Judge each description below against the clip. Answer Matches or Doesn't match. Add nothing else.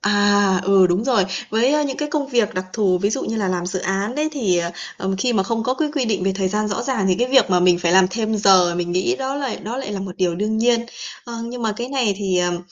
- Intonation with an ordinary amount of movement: Matches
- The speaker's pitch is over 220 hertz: Doesn't match